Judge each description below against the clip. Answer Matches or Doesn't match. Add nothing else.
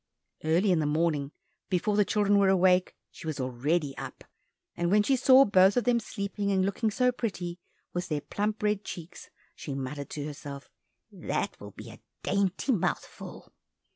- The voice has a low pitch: Doesn't match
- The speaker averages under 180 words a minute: Matches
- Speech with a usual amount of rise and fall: Matches